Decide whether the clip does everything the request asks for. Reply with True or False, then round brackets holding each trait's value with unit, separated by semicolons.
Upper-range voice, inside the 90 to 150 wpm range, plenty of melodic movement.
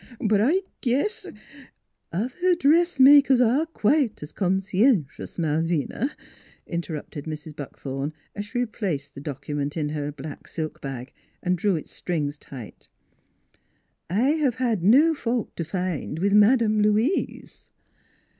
True (195 Hz; 140 wpm; 8.7 semitones)